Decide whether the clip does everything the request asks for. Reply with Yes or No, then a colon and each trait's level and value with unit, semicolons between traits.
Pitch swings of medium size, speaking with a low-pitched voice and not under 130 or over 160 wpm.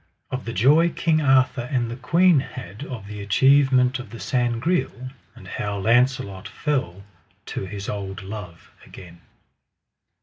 Yes: average, 4.9 semitones; low, 125 Hz; average, 140 wpm